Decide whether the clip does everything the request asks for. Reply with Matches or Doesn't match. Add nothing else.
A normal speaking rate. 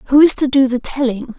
Doesn't match